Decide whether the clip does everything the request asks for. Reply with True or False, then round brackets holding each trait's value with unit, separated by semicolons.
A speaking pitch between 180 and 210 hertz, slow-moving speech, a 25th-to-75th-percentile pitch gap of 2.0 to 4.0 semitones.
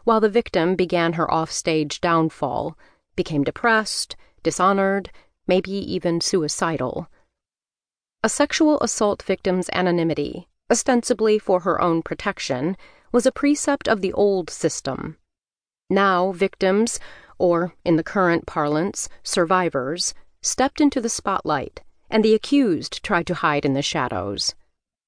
False (185 Hz; 120 wpm; 4.7 semitones)